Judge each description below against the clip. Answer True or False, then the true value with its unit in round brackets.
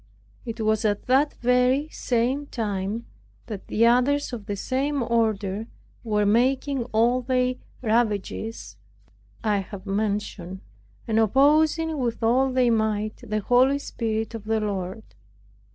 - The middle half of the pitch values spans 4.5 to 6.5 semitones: False (3.2 semitones)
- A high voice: True (230 Hz)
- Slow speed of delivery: True (130 wpm)